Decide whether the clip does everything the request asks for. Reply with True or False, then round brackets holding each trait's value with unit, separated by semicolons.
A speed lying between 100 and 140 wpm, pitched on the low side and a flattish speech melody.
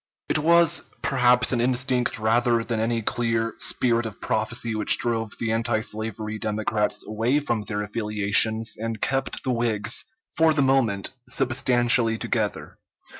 True (135 wpm; 115 Hz; 2.1 semitones)